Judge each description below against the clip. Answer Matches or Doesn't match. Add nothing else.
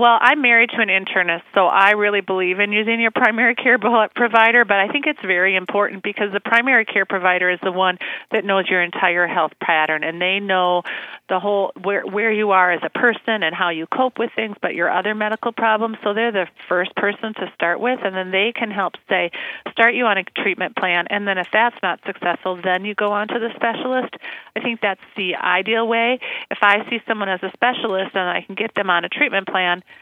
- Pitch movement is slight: Doesn't match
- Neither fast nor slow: Doesn't match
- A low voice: Doesn't match